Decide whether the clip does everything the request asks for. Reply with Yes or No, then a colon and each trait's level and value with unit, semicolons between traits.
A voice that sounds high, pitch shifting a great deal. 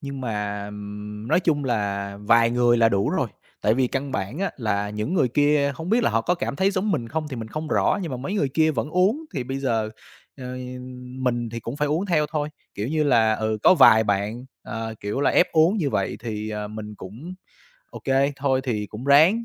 No: low, 130 Hz; wide, 5.7 semitones